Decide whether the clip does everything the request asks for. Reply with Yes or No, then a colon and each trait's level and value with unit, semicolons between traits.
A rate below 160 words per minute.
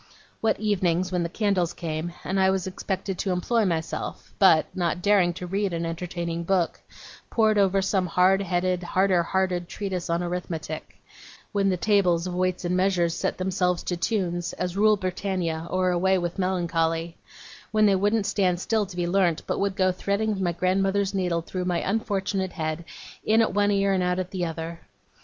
No: average, 185 wpm